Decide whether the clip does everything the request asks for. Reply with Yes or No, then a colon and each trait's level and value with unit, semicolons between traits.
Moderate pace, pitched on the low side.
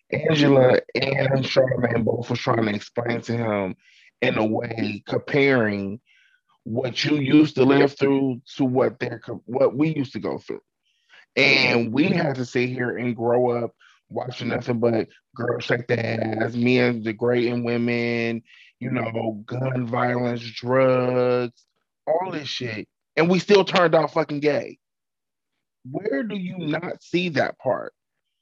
Yes: average, 150 wpm; low, 125 Hz